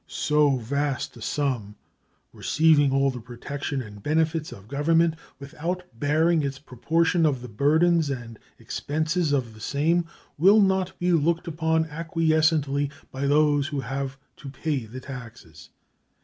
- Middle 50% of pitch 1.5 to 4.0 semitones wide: Yes, average, 3.3 semitones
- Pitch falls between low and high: Yes, medium, 145 Hz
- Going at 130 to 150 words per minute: Yes, average, 140 wpm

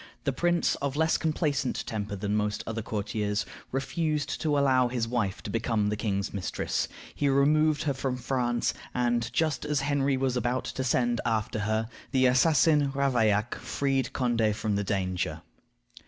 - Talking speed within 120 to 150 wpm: No, average, 160 wpm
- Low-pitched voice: Yes, low, 125 Hz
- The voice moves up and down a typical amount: Yes, average, 4.5 semitones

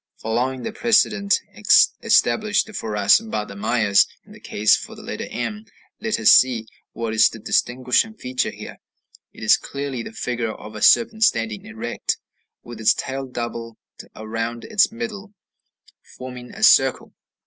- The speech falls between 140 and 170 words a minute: Yes, average, 155 wpm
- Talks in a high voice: No, low, 125 Hz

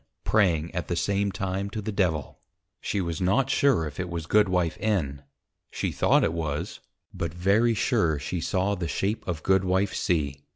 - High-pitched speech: No, very low, 90 Hz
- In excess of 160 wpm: Yes, average, 175 wpm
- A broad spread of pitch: No, average, 3.5 semitones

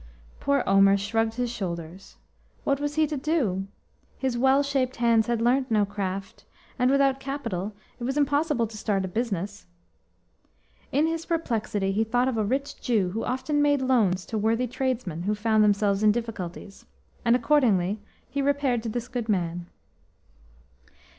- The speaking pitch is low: No, high, 230 Hz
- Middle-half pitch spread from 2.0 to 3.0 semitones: No, average, 4.8 semitones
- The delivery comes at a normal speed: Yes, average, 160 wpm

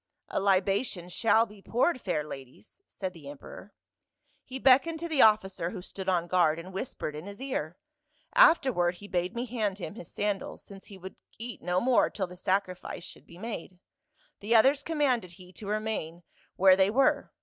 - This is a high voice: Yes, high, 195 Hz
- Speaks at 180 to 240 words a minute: Yes, average, 185 wpm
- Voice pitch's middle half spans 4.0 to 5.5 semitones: Yes, average, 4.6 semitones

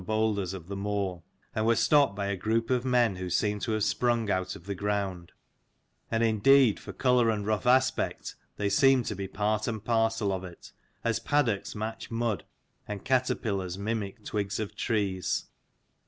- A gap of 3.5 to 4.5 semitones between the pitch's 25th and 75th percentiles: No, average, 2.7 semitones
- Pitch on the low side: Yes, low, 105 Hz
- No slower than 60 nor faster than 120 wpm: No, average, 175 wpm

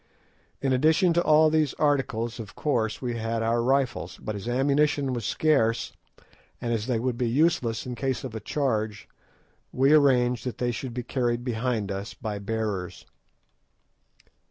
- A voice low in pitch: Yes, low, 120 Hz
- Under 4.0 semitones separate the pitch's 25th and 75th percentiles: Yes, average, 3.4 semitones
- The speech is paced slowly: No, average, 160 wpm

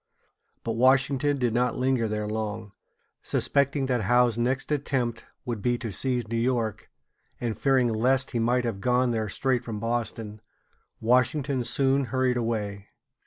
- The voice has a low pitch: Yes, low, 120 Hz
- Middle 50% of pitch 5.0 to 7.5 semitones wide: No, narrow, 2.5 semitones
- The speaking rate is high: No, average, 150 wpm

